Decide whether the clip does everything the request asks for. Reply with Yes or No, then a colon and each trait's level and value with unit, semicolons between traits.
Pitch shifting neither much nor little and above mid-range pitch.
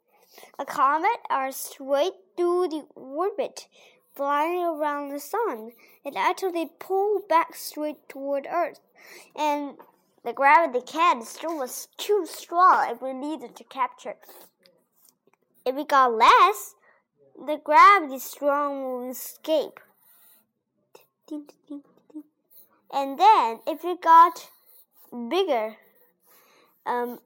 Yes: average, 4.9 semitones; very high, 305 Hz